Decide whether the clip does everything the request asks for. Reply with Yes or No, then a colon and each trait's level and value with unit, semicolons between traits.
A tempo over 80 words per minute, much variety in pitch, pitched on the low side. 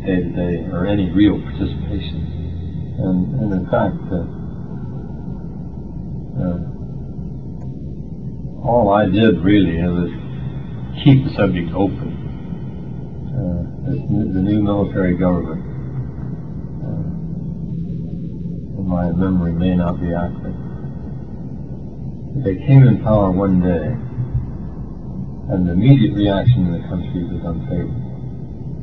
Yes: slow, 105 wpm; wide, 6.9 semitones; low, 100 Hz